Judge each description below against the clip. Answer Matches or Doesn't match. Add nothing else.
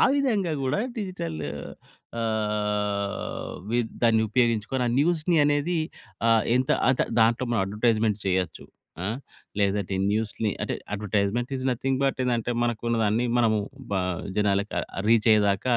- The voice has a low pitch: Matches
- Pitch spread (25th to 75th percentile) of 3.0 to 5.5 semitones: Matches